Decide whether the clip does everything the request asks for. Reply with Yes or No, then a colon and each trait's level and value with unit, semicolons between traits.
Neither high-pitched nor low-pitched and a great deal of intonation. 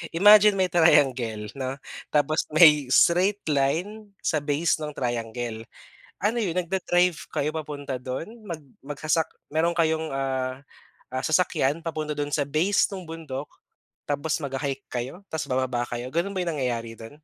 No: medium, 150 Hz; average, 4.5 semitones